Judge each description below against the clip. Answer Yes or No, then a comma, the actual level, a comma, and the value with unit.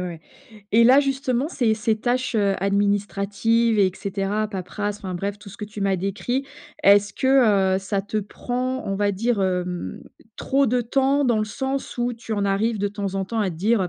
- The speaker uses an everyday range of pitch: Yes, average, 3.4 semitones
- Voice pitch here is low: No, high, 210 Hz